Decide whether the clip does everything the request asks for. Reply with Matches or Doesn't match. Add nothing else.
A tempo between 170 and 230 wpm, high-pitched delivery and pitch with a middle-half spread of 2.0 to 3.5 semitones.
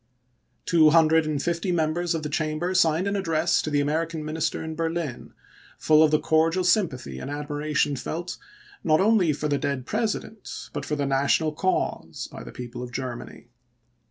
Doesn't match